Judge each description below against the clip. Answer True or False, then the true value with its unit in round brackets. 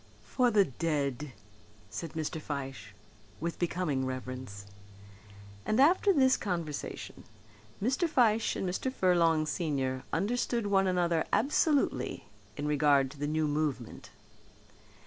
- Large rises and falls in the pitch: True (6.4 semitones)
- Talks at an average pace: False (115 wpm)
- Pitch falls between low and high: True (165 Hz)